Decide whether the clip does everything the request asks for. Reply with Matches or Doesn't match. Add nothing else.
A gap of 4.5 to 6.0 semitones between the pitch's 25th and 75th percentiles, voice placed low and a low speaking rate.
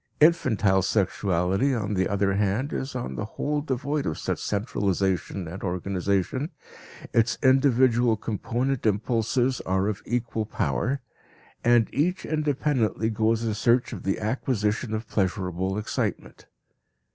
Matches